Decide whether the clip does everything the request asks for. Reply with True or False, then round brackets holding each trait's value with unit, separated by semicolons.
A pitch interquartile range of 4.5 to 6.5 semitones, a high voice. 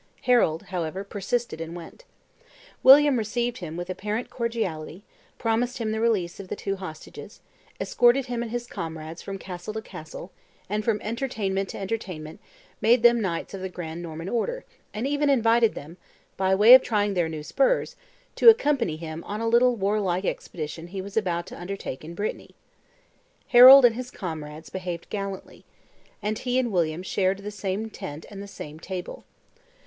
True (5.2 semitones; 200 Hz)